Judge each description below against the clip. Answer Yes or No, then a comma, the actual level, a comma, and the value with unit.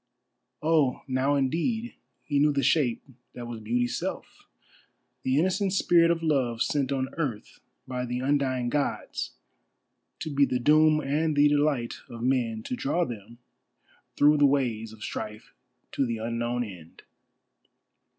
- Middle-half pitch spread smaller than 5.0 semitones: Yes, average, 4.0 semitones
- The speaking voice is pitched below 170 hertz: Yes, low, 135 Hz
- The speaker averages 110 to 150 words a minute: Yes, average, 140 wpm